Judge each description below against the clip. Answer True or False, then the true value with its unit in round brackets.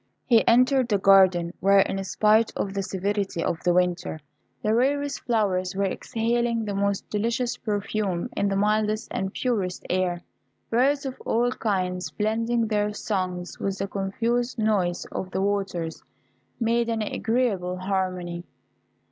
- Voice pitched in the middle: False (200 Hz)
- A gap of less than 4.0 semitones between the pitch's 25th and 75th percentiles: True (3.6 semitones)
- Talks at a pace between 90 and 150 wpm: True (145 wpm)